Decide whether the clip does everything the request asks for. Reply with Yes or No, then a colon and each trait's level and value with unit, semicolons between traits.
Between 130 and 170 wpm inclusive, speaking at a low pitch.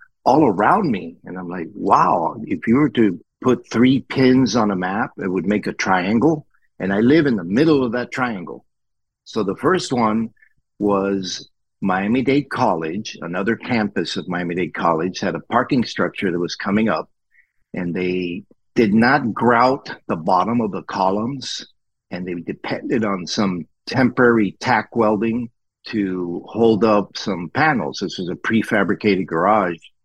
Yes: average, 160 wpm; low, 105 Hz